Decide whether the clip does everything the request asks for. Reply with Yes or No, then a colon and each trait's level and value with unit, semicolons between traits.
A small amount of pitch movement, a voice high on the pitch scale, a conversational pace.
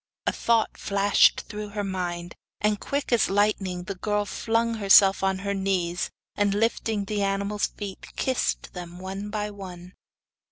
Yes: narrow, 1.7 semitones; high, 200 Hz; average, 155 wpm